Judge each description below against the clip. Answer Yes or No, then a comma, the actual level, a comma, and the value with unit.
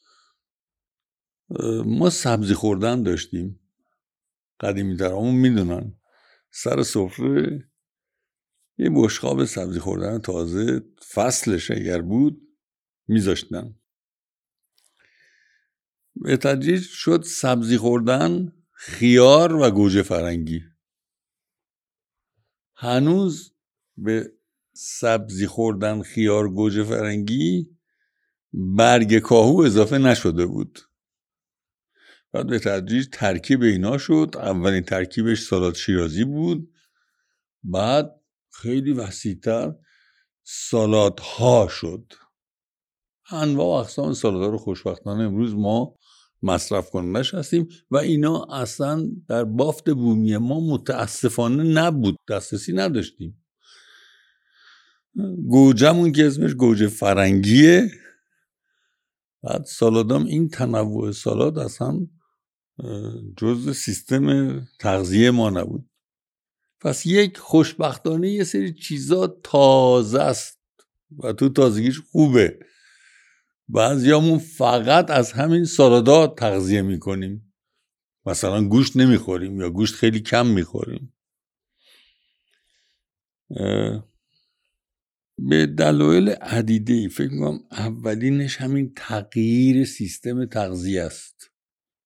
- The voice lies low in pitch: Yes, low, 120 Hz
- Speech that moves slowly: Yes, slow, 85 wpm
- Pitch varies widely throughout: Yes, wide, 6.6 semitones